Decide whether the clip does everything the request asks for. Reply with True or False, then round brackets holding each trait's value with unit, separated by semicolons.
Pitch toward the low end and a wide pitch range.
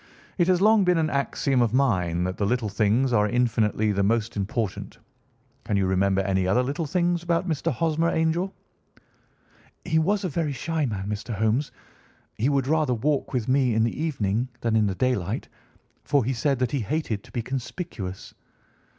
True (125 Hz; 6.7 semitones)